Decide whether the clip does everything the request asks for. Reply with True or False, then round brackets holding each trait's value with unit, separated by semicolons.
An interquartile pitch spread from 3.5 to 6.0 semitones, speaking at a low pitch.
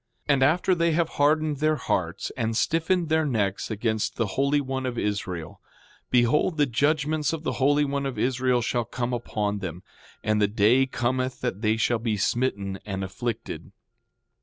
True (5.1 semitones; 125 Hz)